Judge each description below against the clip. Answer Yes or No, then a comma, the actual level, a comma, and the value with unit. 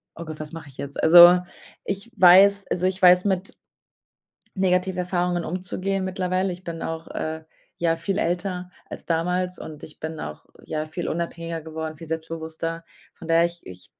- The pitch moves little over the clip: Yes, narrow, 2.1 semitones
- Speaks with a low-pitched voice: No, medium, 170 Hz